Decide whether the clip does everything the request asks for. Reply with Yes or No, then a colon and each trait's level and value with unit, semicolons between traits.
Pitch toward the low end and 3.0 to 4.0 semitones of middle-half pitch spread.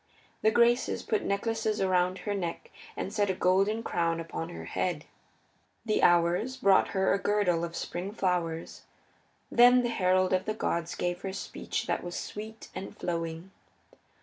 No: high, 190 Hz; average, 3.7 semitones